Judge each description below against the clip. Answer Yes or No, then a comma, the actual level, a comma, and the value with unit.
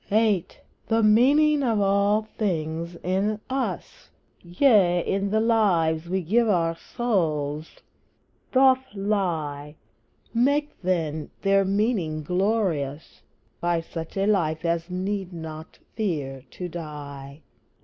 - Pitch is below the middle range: No, medium, 185 Hz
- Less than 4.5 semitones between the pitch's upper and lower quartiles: No, average, 5.0 semitones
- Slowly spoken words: Yes, slow, 110 wpm